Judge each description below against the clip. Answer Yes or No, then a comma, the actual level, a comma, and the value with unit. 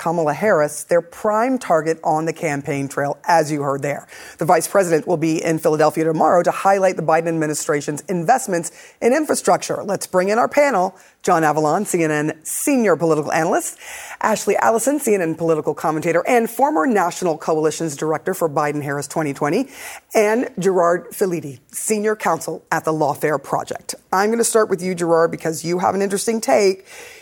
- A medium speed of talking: Yes, average, 165 wpm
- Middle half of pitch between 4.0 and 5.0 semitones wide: Yes, average, 4.6 semitones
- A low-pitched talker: No, medium, 170 Hz